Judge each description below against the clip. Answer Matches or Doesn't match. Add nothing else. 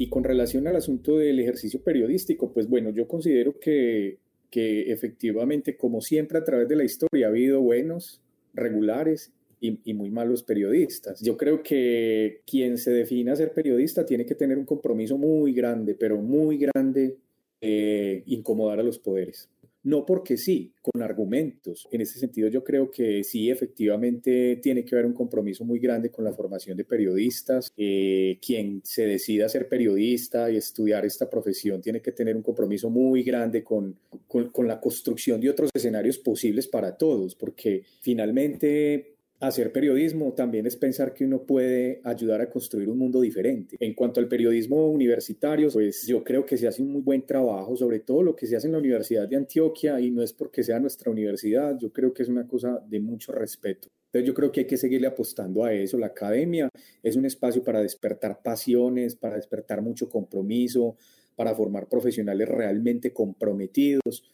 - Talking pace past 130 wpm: Matches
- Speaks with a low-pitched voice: Matches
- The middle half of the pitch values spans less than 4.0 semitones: Matches